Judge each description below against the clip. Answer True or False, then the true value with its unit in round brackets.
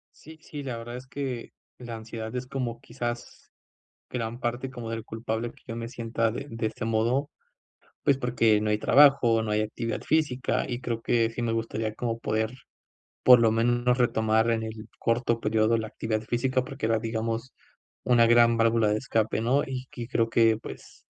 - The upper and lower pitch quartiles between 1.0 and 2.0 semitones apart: True (1.7 semitones)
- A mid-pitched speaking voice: False (115 Hz)